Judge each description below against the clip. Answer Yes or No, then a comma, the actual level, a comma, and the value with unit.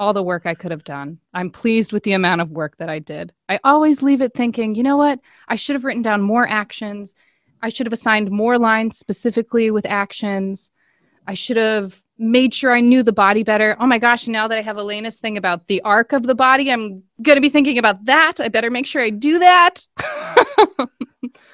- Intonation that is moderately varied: Yes, average, 4.1 semitones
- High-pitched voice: Yes, high, 225 Hz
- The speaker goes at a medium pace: No, fast, 225 wpm